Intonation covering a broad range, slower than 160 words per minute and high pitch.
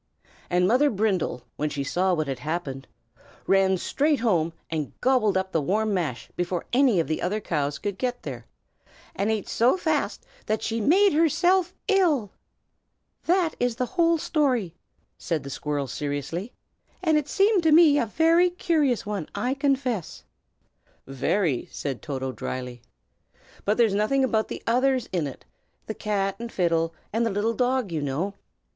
No: wide, 8.6 semitones; average, 165 wpm; high, 210 Hz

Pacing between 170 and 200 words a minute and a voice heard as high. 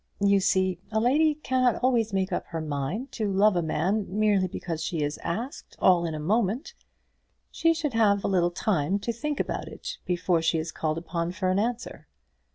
Yes: average, 195 wpm; high, 195 Hz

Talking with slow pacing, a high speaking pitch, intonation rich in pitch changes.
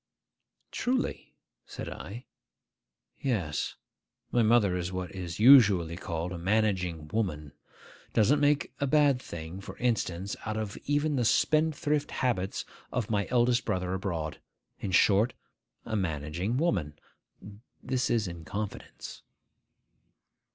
No: slow, 120 wpm; low, 105 Hz; wide, 5.8 semitones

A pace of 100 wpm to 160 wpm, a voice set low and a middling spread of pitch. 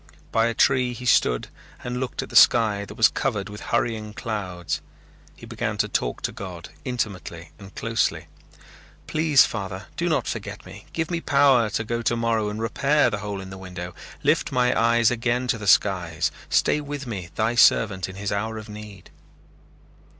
No: average, 180 wpm; low, 110 Hz; average, 3.7 semitones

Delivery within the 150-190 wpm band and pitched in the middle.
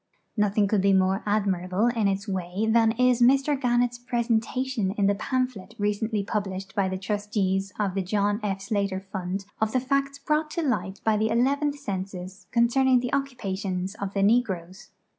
No: average, 180 wpm; high, 210 Hz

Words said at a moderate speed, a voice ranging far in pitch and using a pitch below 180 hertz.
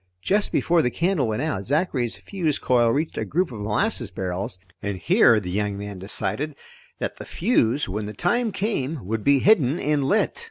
Yes: average, 190 wpm; wide, 8.6 semitones; low, 135 Hz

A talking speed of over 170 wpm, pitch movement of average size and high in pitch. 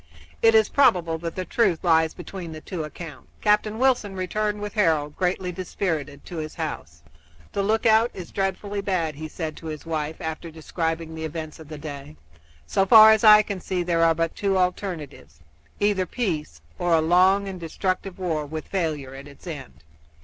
No: average, 185 wpm; average, 3.9 semitones; medium, 170 Hz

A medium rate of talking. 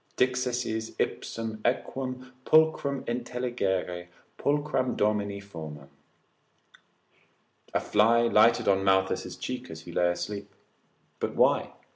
No: slow, 100 wpm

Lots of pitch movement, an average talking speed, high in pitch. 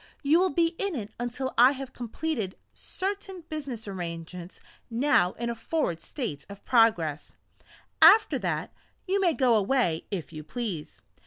Yes: wide, 8.6 semitones; average, 150 wpm; high, 240 Hz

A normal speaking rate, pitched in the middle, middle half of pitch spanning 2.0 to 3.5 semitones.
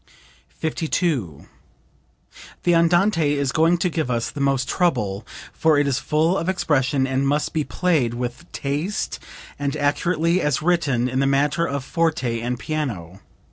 No: average, 150 wpm; medium, 145 Hz; average, 4.2 semitones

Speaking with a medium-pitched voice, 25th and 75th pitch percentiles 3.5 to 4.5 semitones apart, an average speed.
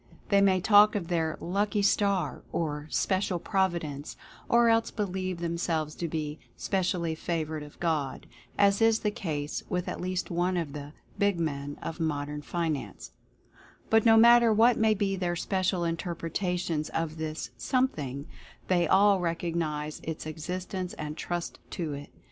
Yes: medium, 175 Hz; average, 3.9 semitones; average, 155 wpm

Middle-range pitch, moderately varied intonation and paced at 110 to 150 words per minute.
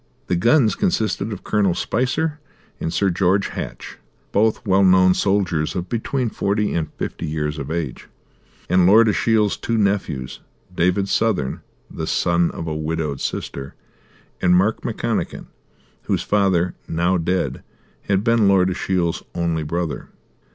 No: very low, 95 Hz; average, 3.7 semitones; average, 140 wpm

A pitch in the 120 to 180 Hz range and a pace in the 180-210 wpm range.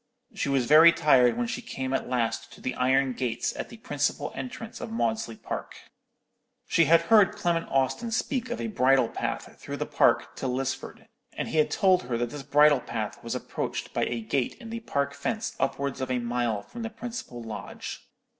Yes: medium, 140 Hz; average, 200 wpm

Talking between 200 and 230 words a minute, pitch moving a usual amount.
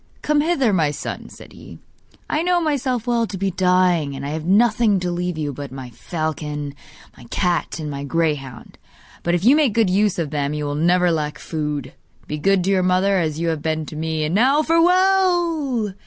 No: fast, 205 wpm; wide, 7.3 semitones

